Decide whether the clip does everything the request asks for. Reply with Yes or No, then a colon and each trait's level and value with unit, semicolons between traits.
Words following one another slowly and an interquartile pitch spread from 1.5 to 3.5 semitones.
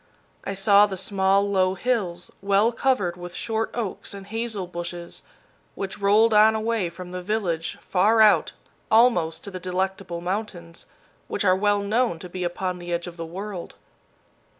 No: average, 165 wpm; average, 3.1 semitones